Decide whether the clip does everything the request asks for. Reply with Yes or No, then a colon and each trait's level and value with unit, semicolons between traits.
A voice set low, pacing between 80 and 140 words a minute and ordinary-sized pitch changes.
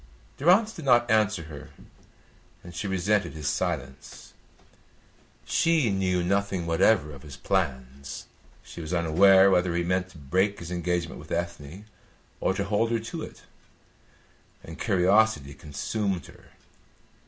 Yes: very low, 90 Hz; slow, 135 wpm; average, 4.0 semitones